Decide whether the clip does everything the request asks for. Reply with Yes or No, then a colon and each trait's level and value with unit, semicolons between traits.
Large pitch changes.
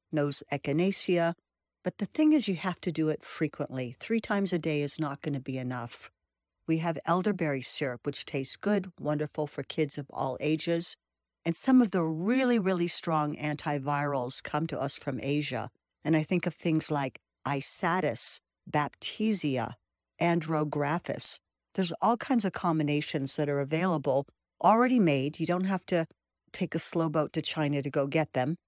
No: average, 3.6 semitones